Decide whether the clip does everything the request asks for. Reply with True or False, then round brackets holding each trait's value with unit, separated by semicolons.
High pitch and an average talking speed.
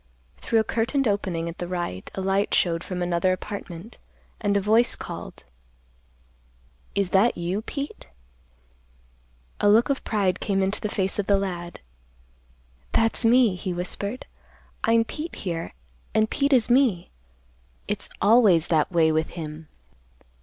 True (195 Hz; 145 wpm)